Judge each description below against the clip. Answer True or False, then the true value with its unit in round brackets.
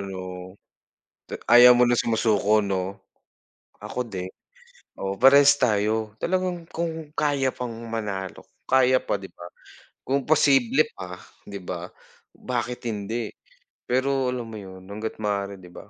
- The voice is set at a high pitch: False (115 Hz)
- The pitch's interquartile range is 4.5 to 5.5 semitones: True (4.8 semitones)